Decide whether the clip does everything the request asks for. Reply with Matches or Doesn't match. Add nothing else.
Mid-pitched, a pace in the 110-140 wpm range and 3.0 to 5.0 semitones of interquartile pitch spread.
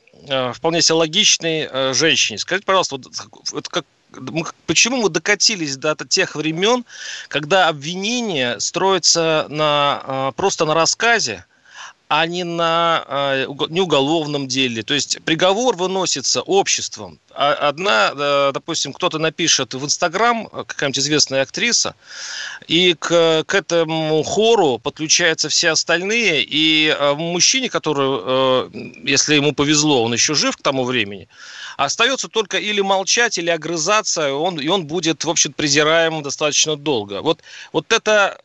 Matches